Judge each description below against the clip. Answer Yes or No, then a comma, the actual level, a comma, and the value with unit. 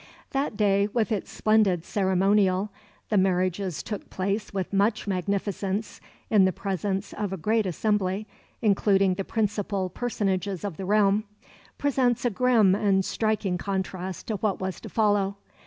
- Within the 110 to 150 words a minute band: Yes, average, 145 wpm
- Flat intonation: Yes, narrow, 2.0 semitones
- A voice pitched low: No, high, 200 Hz